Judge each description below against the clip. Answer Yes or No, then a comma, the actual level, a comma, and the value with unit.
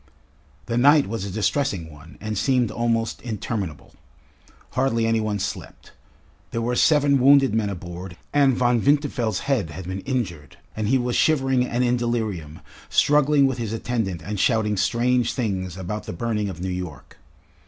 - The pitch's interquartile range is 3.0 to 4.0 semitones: No, average, 4.8 semitones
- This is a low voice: Yes, low, 115 Hz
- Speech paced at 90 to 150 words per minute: No, average, 165 wpm